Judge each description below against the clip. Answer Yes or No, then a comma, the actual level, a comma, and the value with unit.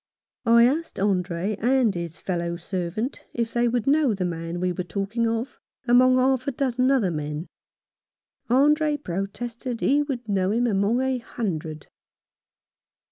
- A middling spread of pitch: No, wide, 5.8 semitones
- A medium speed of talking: Yes, average, 145 wpm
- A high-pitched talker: Yes, high, 230 Hz